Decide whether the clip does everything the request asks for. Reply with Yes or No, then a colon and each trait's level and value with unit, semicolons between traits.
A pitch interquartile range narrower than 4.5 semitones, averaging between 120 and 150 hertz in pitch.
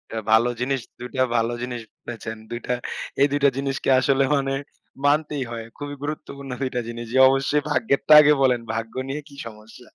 Yes: average, 2.9 semitones; low, 135 Hz